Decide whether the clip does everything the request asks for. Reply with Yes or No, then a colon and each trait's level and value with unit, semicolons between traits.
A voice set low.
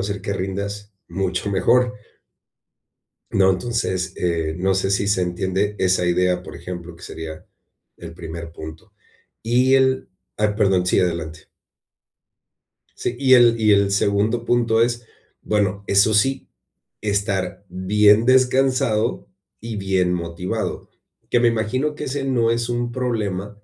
Yes: low, 100 Hz